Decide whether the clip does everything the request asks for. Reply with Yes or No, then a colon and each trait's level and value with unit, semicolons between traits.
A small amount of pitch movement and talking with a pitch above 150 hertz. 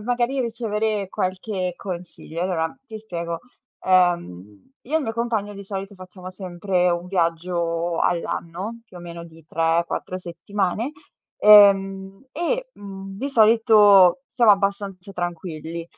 No: average, 3.6 semitones; high, 190 Hz